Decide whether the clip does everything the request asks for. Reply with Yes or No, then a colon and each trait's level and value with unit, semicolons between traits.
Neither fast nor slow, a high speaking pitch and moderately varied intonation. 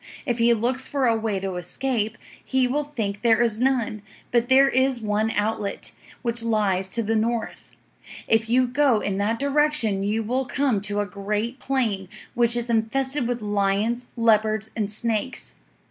Yes: average, 170 wpm; high, 230 Hz; average, 3.1 semitones